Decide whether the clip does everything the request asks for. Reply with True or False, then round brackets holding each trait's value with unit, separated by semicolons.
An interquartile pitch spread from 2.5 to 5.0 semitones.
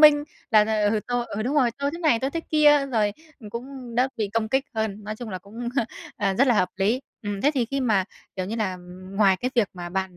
True (4.6 semitones)